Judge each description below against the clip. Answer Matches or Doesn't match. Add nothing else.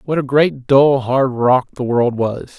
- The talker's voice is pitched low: Matches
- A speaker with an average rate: Doesn't match